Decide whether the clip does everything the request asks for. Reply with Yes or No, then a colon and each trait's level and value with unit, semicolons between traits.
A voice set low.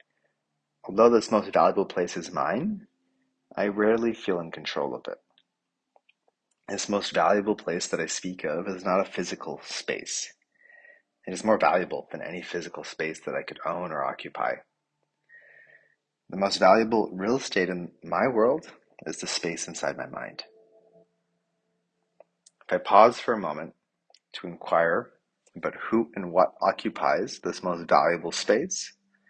Yes: low, 115 Hz